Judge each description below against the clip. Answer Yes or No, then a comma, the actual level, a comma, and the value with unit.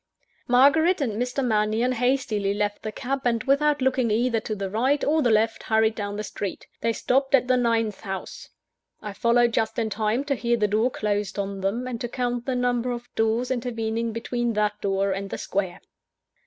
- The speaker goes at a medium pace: Yes, average, 195 wpm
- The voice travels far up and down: No, average, 2.9 semitones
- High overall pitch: Yes, high, 230 Hz